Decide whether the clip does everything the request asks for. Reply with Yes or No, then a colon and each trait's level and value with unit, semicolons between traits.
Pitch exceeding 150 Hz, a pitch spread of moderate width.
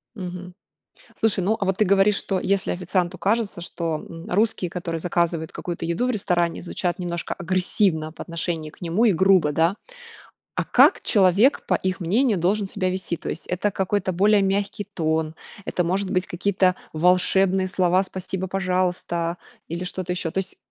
No: medium, 185 Hz; narrow, 2.2 semitones